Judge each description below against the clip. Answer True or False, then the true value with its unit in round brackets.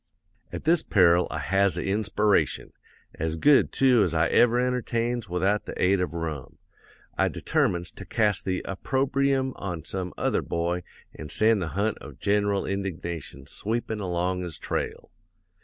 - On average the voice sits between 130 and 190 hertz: False (100 Hz)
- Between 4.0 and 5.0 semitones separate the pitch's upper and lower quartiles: True (4.6 semitones)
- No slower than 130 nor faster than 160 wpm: True (155 wpm)